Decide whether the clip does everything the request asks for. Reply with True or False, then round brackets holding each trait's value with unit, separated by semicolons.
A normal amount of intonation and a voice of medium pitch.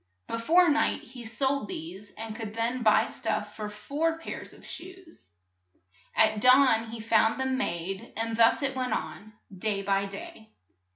False (3.9 semitones; 225 Hz)